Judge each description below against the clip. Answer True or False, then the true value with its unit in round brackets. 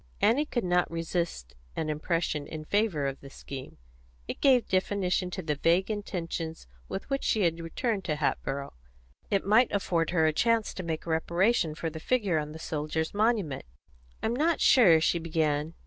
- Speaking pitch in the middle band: True (170 Hz)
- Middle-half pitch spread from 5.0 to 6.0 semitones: False (4.6 semitones)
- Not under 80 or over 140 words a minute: False (175 wpm)